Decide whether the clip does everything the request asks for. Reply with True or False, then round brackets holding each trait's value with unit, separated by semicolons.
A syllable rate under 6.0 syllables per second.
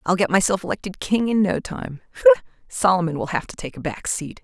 False (6.3 syllables/s)